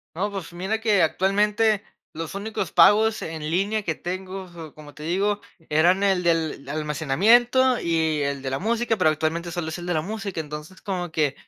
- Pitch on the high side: No, medium, 175 Hz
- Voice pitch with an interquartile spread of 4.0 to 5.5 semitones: Yes, average, 4.5 semitones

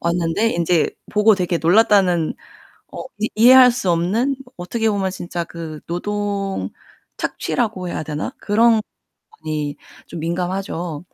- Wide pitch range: No, average, 4.0 semitones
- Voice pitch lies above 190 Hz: No, medium, 185 Hz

